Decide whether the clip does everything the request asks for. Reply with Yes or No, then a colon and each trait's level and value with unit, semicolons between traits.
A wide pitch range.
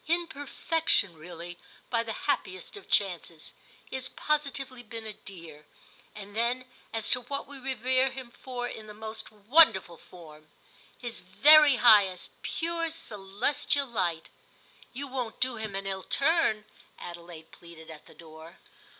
Yes: wide, 6.5 semitones